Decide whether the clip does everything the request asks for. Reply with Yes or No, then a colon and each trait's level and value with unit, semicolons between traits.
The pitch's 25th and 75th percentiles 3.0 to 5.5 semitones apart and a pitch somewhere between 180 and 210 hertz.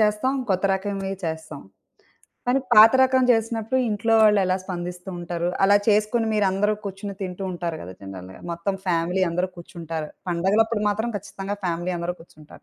Yes: average, 3.6 semitones; high, 190 Hz